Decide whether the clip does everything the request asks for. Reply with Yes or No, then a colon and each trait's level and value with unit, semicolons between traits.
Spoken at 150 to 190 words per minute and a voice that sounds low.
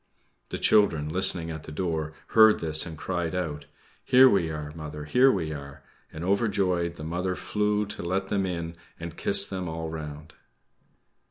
Yes: average, 170 wpm; very low, 85 Hz